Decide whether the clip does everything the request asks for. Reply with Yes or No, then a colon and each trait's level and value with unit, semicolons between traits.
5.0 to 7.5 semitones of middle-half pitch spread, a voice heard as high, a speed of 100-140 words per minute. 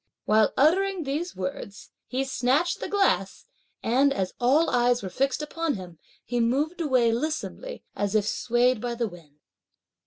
No: wide, 5.6 semitones; very high, 250 Hz; average, 155 wpm